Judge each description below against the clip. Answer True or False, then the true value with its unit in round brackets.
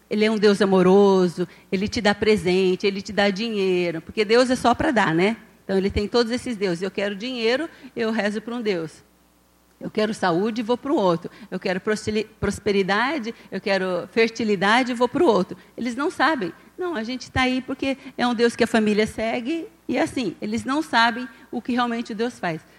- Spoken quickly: True (205 wpm)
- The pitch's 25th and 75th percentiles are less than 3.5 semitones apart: False (3.9 semitones)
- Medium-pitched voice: False (220 Hz)